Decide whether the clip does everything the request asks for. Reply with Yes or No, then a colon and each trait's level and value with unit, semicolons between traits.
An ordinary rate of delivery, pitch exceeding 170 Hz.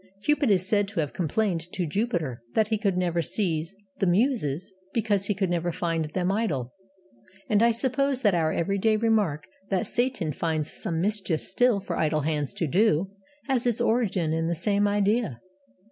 Yes: average, 175 wpm; high, 190 Hz